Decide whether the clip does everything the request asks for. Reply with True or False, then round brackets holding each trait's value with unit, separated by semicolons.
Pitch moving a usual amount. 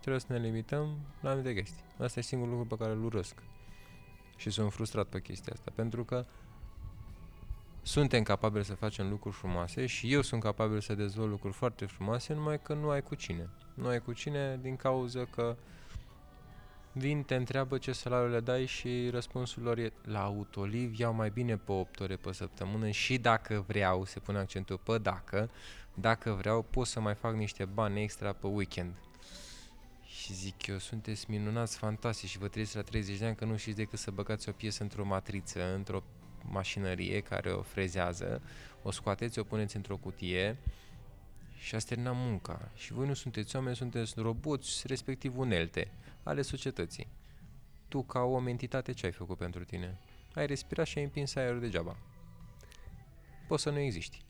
True (4.0 semitones)